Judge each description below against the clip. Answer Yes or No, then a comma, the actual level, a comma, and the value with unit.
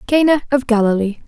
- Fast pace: No, average, 140 wpm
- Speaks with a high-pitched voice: Yes, high, 245 Hz